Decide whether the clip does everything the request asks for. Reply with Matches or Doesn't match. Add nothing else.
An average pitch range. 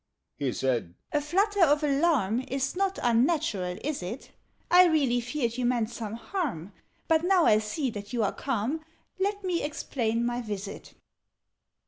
Doesn't match